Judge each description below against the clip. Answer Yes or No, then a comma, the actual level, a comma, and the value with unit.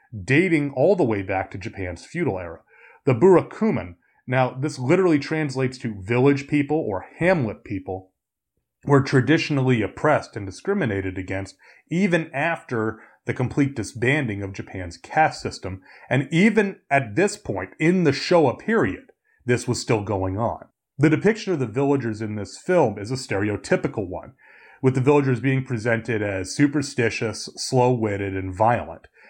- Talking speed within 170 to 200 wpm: No, average, 145 wpm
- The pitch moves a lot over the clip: Yes, wide, 6.1 semitones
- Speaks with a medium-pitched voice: No, low, 130 Hz